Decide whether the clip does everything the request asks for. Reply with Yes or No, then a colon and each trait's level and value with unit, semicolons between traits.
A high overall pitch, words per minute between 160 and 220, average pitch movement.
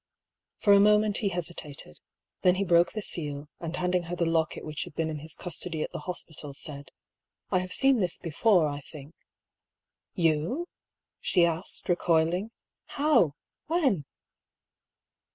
No: medium, 170 Hz; average, 170 wpm; average, 3.7 semitones